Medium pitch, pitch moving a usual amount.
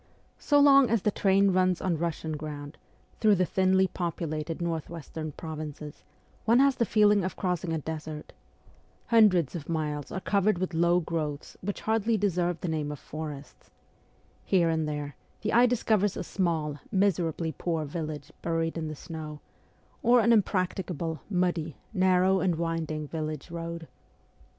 Yes: medium, 170 Hz; average, 3.5 semitones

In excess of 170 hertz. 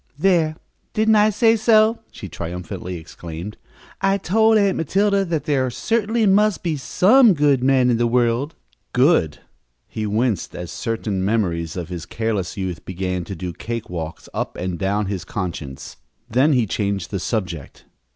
No: low, 115 Hz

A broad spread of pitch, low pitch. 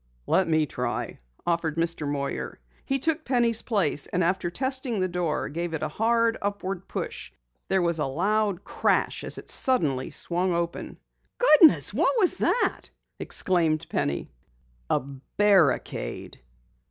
No: wide, 6.1 semitones; medium, 180 Hz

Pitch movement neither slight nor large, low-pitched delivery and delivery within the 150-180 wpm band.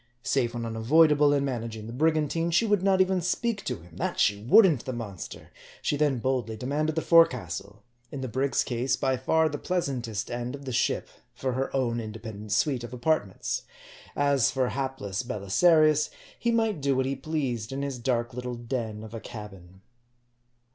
No: average, 4.7 semitones; low, 130 Hz; average, 190 wpm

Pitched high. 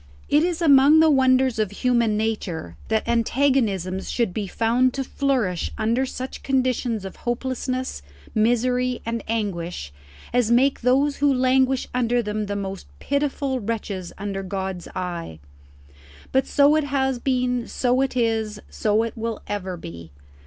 Yes: high, 235 Hz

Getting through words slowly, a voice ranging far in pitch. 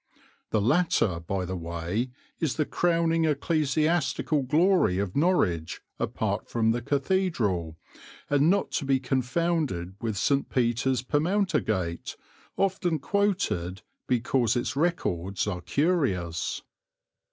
Yes: slow, 110 wpm; wide, 9.0 semitones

